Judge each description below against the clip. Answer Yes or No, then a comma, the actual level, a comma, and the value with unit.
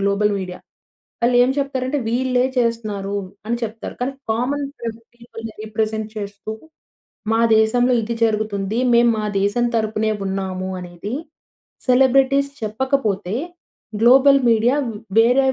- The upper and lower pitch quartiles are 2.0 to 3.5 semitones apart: Yes, average, 3.2 semitones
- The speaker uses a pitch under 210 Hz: No, high, 225 Hz